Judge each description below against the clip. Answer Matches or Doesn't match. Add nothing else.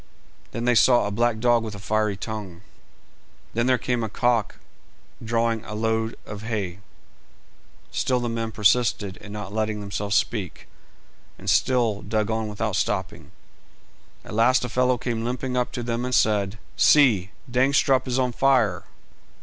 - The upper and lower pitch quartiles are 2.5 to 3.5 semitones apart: Matches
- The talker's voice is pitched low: Matches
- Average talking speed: Matches